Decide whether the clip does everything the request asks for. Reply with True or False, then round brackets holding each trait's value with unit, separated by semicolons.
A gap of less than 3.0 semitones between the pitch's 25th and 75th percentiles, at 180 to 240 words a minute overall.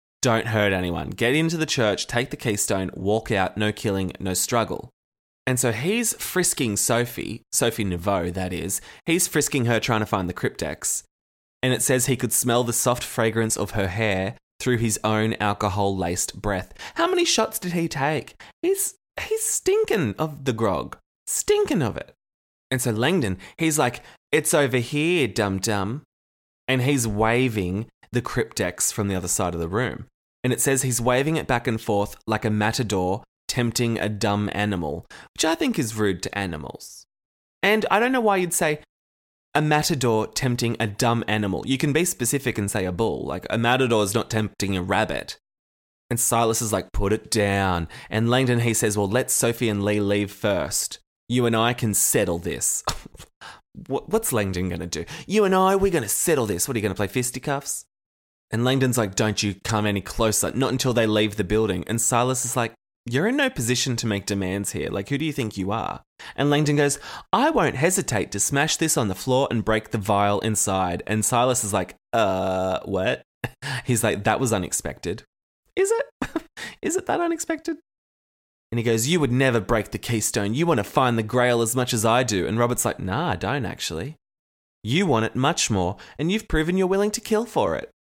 False (5.1 semitones; 200 wpm)